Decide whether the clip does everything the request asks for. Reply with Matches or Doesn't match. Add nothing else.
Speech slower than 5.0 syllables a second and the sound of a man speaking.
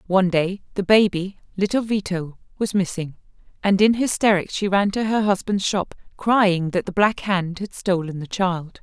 Doesn't match